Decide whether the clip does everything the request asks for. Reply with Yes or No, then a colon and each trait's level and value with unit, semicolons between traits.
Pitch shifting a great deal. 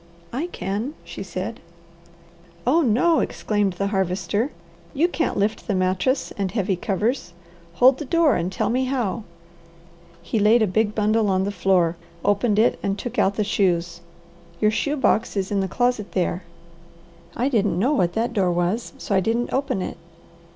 No: average, 4.3 semitones